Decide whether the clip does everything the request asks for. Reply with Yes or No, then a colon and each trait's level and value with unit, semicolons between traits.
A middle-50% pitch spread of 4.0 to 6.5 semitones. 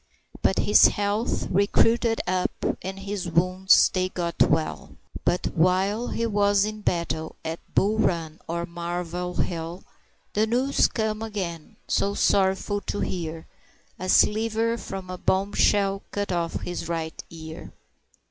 No: average, 3.2 semitones